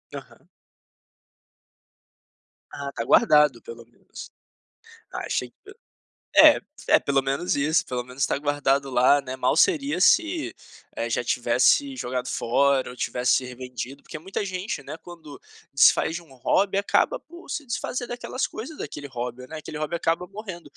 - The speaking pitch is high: No, medium, 145 Hz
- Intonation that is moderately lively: No, wide, 7.0 semitones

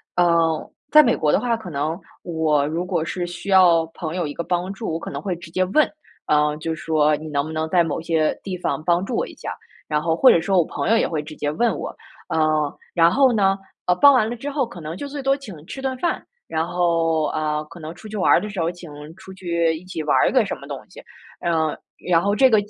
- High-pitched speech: No, medium, 170 Hz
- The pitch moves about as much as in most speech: Yes, average, 3.7 semitones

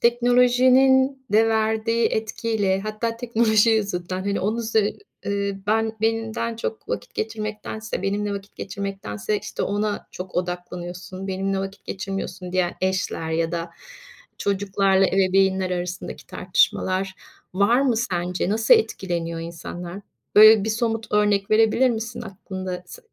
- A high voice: Yes, high, 200 Hz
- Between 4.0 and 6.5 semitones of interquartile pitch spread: No, average, 3.0 semitones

